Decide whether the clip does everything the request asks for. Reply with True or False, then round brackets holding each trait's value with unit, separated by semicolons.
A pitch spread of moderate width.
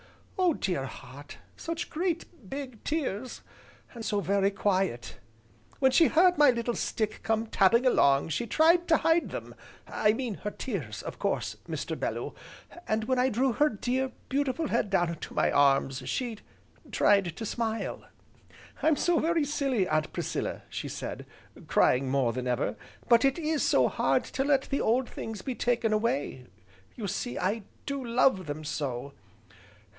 False (6.8 semitones)